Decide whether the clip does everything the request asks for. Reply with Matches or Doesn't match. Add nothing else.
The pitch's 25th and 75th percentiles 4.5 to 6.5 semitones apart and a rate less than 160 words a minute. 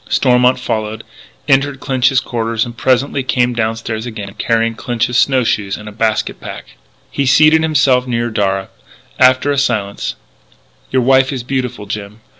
Doesn't match